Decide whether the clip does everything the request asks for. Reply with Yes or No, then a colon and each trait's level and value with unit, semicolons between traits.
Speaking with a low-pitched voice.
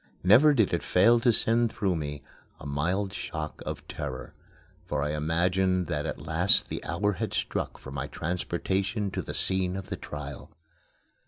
Yes: very low, 90 Hz